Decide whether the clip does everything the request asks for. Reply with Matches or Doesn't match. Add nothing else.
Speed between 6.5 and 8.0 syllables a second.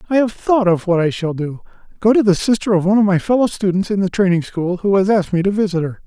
Matches